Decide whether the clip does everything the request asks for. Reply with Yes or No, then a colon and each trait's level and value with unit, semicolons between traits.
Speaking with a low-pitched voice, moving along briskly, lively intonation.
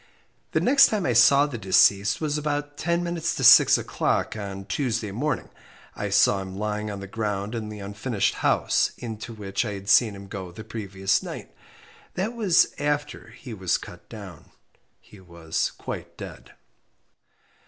No: low, 105 Hz; average, 165 wpm; wide, 6.7 semitones